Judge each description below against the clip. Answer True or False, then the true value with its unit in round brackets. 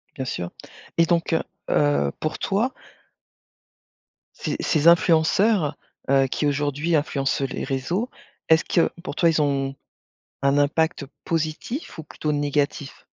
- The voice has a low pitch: False (150 Hz)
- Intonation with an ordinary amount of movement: True (3.0 semitones)